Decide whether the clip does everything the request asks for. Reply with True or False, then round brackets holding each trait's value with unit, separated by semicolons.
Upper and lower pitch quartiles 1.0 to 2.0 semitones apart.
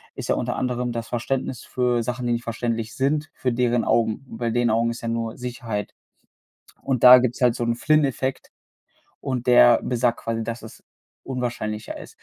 True (1.4 semitones)